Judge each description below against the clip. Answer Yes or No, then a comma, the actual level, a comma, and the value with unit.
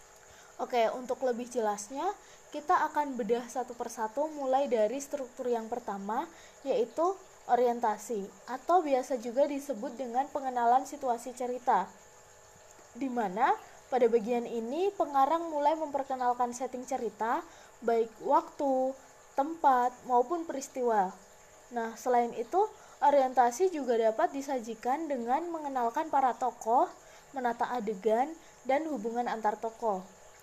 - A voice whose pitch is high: Yes, very high, 255 Hz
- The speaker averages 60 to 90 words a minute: No, average, 110 wpm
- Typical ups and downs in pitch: Yes, average, 3.2 semitones